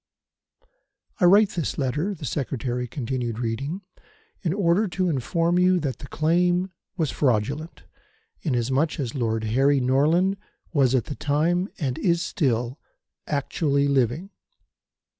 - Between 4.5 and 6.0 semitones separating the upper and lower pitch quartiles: Yes, wide, 5.4 semitones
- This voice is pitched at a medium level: Yes, medium, 145 Hz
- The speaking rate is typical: No, slow, 125 wpm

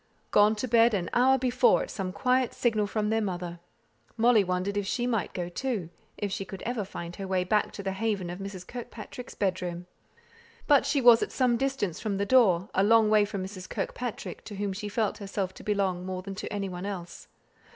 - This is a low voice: No, high, 205 Hz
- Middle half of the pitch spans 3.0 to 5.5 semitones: Yes, average, 3.4 semitones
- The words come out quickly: Yes, fast, 215 wpm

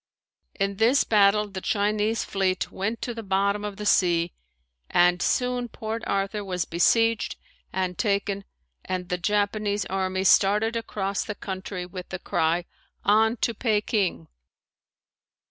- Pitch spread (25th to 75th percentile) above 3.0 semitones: No, narrow, 2.4 semitones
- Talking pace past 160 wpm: No, slow, 135 wpm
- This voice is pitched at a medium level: No, high, 200 Hz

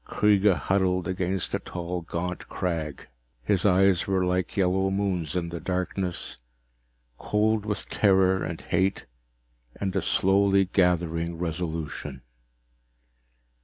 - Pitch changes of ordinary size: No, narrow, 2.2 semitones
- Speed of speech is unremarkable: No, slow, 115 wpm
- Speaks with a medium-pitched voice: No, very low, 90 Hz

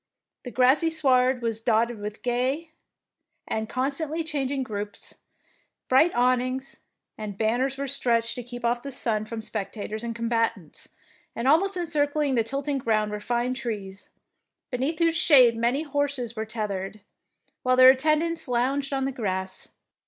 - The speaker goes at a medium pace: Yes, average, 150 wpm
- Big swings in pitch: No, average, 3.6 semitones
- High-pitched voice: Yes, very high, 250 Hz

